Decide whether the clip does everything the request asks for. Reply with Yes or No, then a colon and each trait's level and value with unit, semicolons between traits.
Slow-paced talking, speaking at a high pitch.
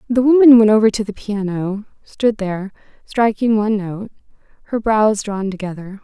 Yes: slow, 130 wpm; high, 210 Hz